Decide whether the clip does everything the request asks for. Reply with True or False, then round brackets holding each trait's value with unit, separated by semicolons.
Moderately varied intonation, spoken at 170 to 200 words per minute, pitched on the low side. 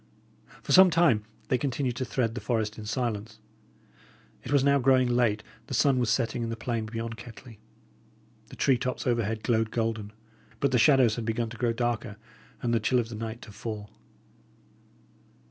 False (2.3 semitones; 180 wpm; 115 Hz)